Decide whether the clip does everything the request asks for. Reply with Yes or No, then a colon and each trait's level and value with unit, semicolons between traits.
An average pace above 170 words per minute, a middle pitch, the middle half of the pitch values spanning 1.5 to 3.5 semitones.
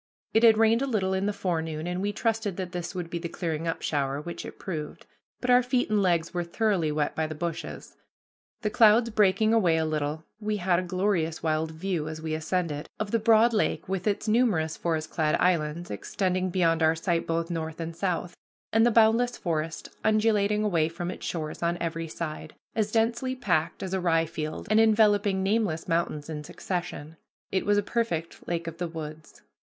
No: average, 200 wpm; medium, 175 Hz; average, 4.6 semitones